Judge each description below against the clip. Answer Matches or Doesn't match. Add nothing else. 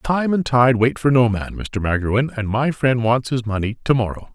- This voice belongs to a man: Matches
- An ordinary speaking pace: Doesn't match